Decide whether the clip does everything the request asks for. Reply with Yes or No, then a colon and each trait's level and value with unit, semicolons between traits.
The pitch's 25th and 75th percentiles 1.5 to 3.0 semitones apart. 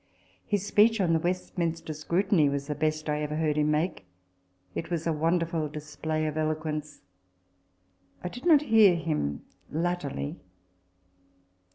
Yes: average, 2.7 semitones